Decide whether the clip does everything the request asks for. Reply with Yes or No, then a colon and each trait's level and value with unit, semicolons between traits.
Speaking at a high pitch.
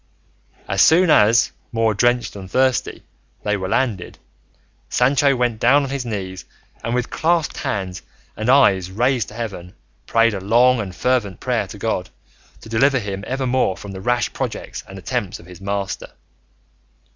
No: low, 115 Hz